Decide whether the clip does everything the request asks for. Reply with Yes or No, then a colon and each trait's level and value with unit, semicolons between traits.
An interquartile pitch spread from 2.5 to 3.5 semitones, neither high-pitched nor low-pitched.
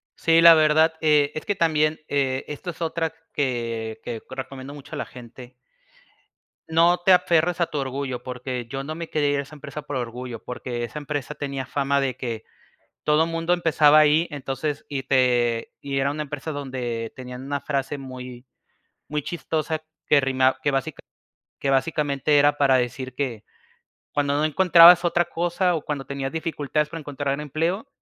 Yes: average, 3.1 semitones; medium, 145 Hz